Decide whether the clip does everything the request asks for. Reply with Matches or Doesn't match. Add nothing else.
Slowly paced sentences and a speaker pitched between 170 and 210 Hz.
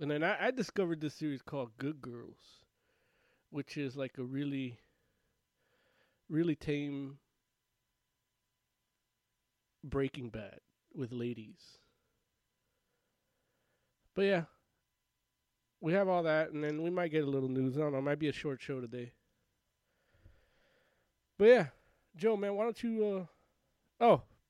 Doesn't match